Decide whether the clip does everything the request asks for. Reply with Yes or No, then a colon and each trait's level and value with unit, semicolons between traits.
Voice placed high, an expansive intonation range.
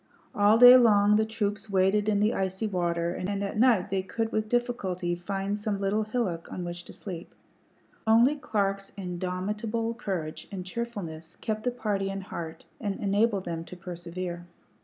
No: high, 200 Hz; average, 3.0 semitones